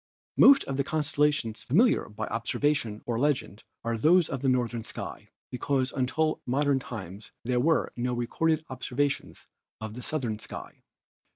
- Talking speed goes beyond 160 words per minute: No, average, 155 wpm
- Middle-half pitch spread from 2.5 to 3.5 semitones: No, average, 4.0 semitones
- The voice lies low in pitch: Yes, low, 130 Hz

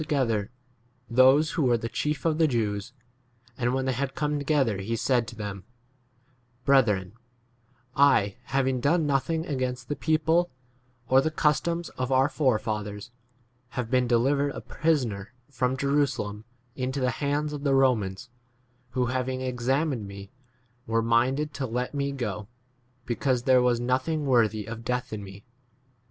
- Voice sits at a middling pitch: No, low, 130 Hz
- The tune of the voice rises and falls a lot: No, average, 3.6 semitones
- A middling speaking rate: Yes, average, 155 wpm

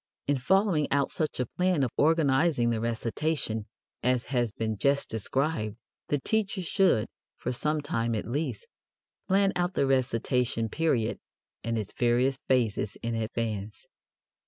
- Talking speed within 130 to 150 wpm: Yes, average, 140 wpm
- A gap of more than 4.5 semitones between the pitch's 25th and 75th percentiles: Yes, average, 5.3 semitones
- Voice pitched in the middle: No, low, 130 Hz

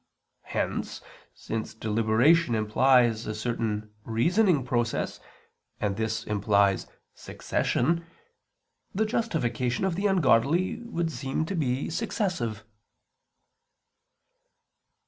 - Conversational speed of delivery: No, slow, 90 wpm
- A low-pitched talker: Yes, low, 125 Hz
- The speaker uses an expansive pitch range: Yes, wide, 7.3 semitones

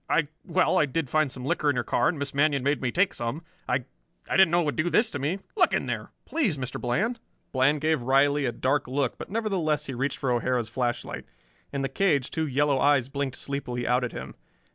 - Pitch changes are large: No, average, 3.4 semitones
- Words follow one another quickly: Yes, fast, 230 wpm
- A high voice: No, medium, 140 Hz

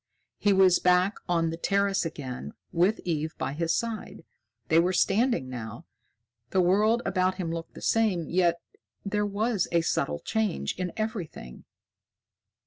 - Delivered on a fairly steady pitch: No, average, 3.6 semitones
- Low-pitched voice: No, medium, 180 Hz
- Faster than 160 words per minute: No, average, 145 wpm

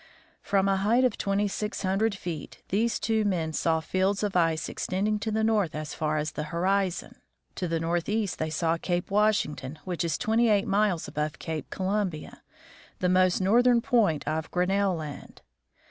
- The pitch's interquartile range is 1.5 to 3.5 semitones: No, average, 4.3 semitones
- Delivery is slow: No, average, 175 wpm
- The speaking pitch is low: No, medium, 185 Hz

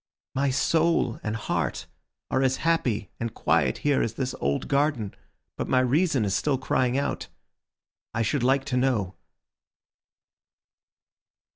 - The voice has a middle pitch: No, low, 130 Hz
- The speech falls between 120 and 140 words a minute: Yes, slow, 135 wpm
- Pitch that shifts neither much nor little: Yes, average, 3.6 semitones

